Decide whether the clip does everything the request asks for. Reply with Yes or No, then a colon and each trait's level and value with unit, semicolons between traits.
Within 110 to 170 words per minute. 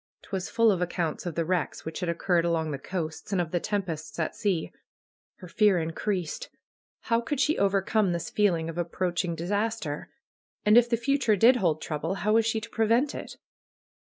No: average, 185 wpm